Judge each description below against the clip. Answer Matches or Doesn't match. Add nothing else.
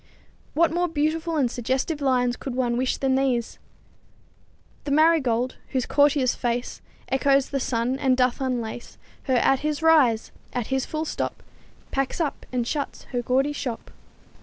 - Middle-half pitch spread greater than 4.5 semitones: Doesn't match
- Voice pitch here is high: Matches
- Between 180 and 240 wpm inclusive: Doesn't match